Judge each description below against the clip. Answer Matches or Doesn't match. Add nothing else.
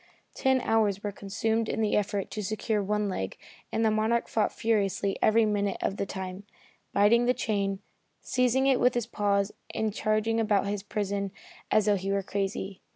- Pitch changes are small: Matches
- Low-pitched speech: Doesn't match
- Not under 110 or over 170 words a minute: Doesn't match